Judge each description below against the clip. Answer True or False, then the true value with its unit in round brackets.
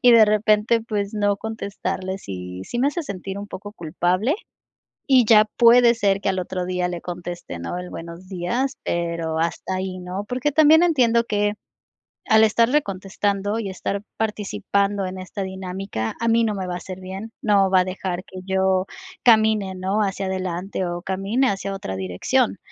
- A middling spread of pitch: True (3.0 semitones)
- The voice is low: False (195 Hz)